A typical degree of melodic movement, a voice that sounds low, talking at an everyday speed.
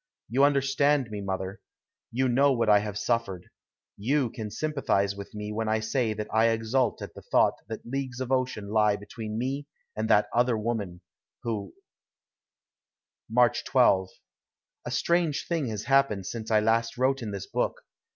Yes: average, 3.8 semitones; low, 115 Hz; average, 165 wpm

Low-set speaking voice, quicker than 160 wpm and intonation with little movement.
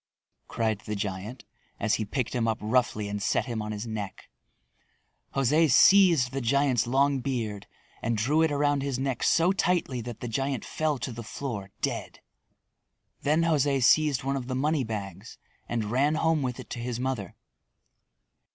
No: low, 125 Hz; average, 170 wpm; average, 4.2 semitones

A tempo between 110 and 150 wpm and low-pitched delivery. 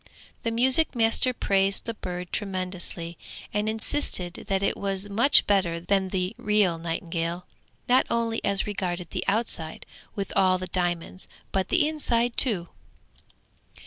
No: average, 140 wpm; high, 195 Hz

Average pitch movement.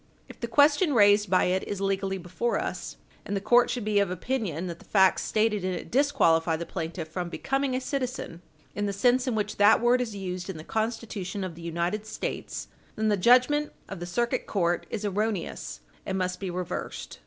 Yes: average, 4.6 semitones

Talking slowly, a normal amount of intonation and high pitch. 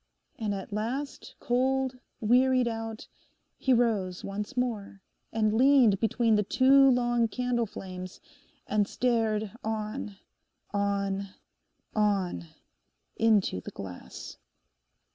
Yes: slow, 95 wpm; average, 3.6 semitones; high, 220 Hz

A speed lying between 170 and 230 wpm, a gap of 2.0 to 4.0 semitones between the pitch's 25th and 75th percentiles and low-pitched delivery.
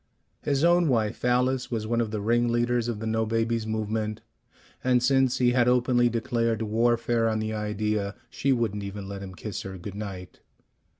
Yes: average, 180 wpm; narrow, 2.4 semitones; low, 115 Hz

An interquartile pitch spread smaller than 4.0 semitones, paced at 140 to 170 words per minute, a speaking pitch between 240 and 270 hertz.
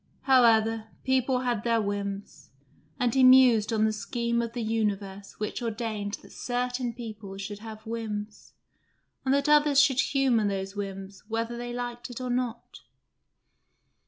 No: average, 2.9 semitones; average, 150 wpm; high, 230 Hz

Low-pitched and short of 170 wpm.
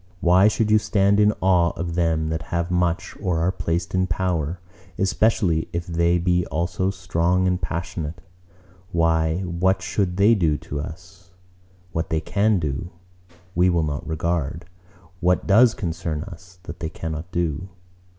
Yes: very low, 85 Hz; average, 155 wpm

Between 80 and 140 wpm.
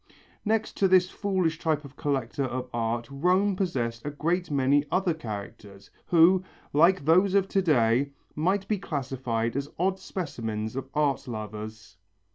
No: average, 150 wpm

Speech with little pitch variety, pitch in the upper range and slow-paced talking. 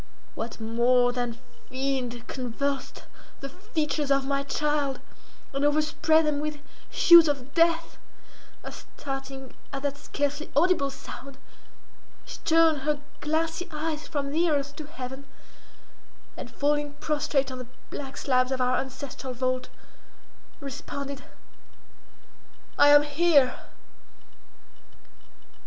Yes: narrow, 2.3 semitones; very high, 280 Hz; slow, 110 wpm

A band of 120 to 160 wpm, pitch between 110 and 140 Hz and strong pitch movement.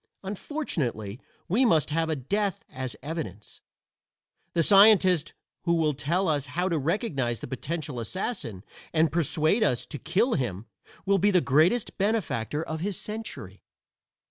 No: average, 145 wpm; medium, 165 Hz; wide, 6.3 semitones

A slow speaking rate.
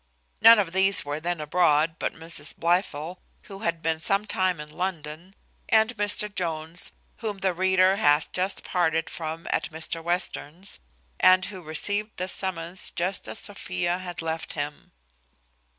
No: average, 150 wpm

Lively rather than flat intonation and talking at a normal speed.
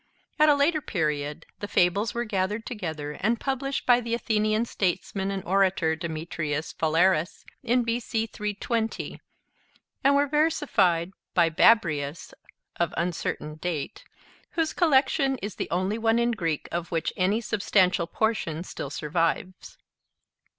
No: wide, 5.9 semitones; slow, 130 wpm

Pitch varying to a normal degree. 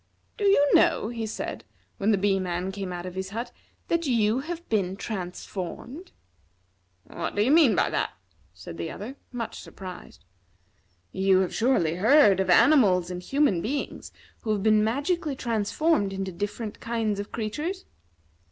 No: wide, 5.7 semitones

